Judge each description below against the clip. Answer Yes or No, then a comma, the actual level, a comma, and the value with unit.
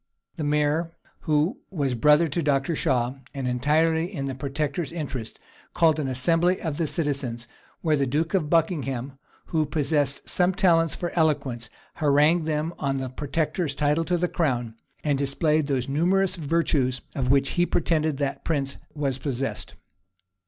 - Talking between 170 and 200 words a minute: No, average, 155 wpm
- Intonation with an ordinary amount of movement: Yes, average, 3.2 semitones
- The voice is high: No, medium, 150 Hz